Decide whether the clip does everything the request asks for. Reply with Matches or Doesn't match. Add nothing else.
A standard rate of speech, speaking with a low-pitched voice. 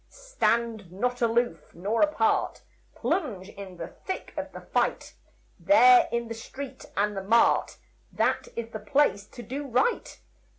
Doesn't match